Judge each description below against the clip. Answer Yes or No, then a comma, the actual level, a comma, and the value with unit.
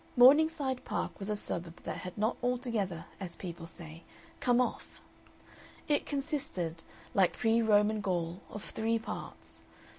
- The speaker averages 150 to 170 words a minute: No, average, 140 wpm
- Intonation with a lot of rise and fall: Yes, wide, 6.0 semitones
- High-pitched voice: Yes, high, 210 Hz